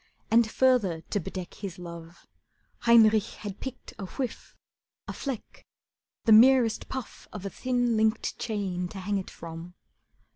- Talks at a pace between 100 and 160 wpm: Yes, average, 145 wpm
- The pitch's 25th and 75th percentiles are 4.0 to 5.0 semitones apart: Yes, average, 4.3 semitones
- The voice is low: No, high, 210 Hz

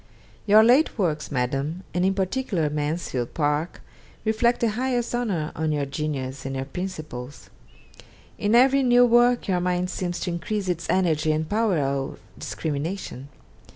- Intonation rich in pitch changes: Yes, wide, 6.6 semitones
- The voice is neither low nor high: Yes, medium, 175 Hz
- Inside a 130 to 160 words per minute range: Yes, average, 150 wpm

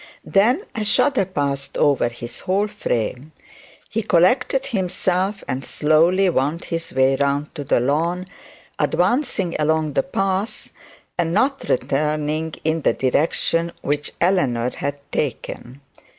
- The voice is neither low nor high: Yes, medium, 160 Hz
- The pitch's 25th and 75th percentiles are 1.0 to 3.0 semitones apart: No, average, 5.2 semitones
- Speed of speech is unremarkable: No, slow, 125 wpm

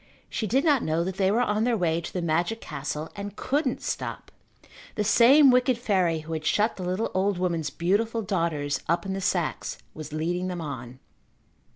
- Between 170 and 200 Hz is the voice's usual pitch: Yes, medium, 185 Hz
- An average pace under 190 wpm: No, average, 195 wpm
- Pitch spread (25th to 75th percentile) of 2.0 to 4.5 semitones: No, average, 5.0 semitones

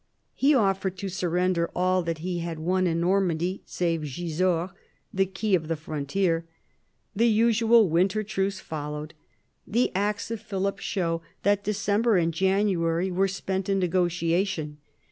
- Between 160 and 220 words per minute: No, average, 145 wpm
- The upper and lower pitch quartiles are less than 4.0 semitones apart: Yes, average, 2.8 semitones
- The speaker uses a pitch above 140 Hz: Yes, medium, 185 Hz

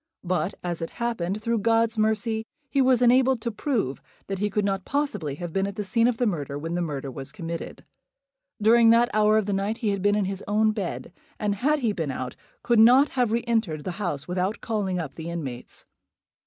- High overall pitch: Yes, high, 205 Hz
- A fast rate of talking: Yes, fast, 220 wpm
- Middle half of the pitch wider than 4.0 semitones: Yes, average, 4.8 semitones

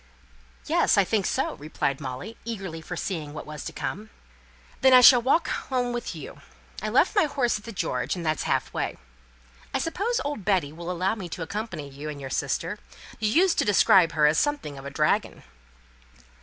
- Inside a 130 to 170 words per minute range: No, average, 195 wpm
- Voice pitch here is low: No, high, 190 Hz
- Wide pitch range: Yes, wide, 7.9 semitones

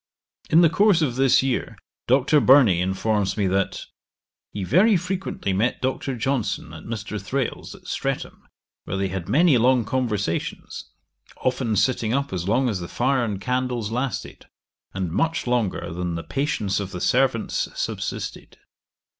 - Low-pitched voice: Yes, low, 120 Hz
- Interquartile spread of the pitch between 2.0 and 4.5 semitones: No, wide, 5.5 semitones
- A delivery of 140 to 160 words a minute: Yes, average, 155 wpm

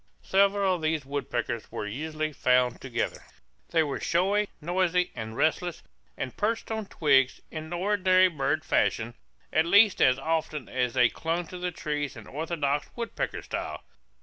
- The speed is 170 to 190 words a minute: No, average, 150 wpm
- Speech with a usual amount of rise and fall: Yes, average, 4.9 semitones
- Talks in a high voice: No, medium, 160 Hz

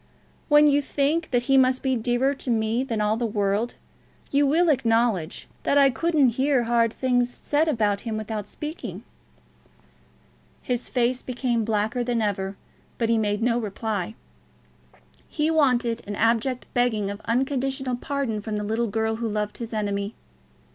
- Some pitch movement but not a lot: Yes, average, 3.5 semitones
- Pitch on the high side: Yes, high, 240 Hz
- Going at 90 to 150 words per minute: No, average, 160 wpm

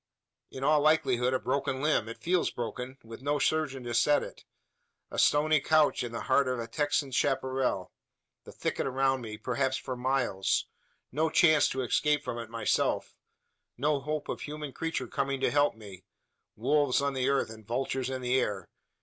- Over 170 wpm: Yes, average, 185 wpm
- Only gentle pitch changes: No, average, 3.2 semitones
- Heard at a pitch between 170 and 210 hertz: No, low, 130 Hz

